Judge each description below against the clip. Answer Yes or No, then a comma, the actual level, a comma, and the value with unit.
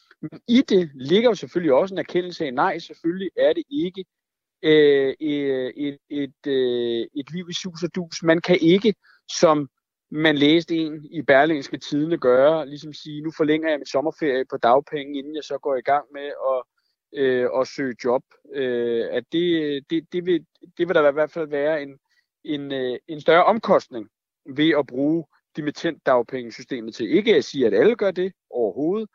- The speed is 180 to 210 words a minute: Yes, average, 185 wpm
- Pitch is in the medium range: Yes, medium, 155 Hz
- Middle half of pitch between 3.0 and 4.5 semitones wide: Yes, average, 3.5 semitones